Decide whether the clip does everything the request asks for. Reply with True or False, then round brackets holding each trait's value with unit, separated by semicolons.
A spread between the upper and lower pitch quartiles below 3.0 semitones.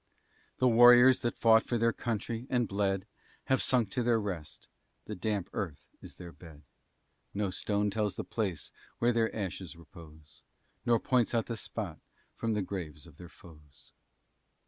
False (5.1 semitones)